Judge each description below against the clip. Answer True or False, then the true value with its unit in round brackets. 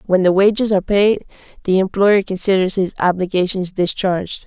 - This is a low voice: False (190 Hz)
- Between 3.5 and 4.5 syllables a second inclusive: False (5.4 syllables/s)